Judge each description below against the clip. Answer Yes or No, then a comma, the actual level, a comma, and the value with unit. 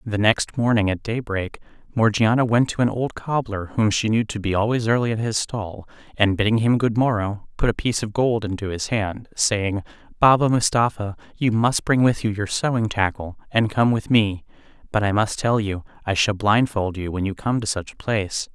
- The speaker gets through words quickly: Yes, fast, 210 wpm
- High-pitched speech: No, low, 110 Hz